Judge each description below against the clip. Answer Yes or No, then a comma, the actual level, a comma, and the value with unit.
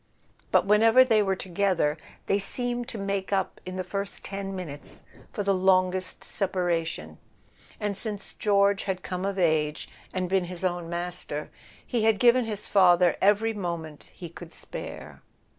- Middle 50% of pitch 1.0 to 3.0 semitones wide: Yes, narrow, 2.5 semitones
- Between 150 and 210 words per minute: Yes, average, 160 wpm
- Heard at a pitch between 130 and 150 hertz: No, high, 190 Hz